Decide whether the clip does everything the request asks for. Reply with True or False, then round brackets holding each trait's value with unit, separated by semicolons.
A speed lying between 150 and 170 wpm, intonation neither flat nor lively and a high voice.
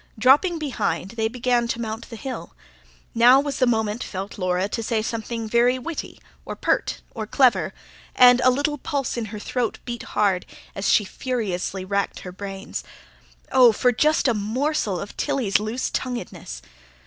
True (165 wpm; 3.7 semitones; 230 Hz)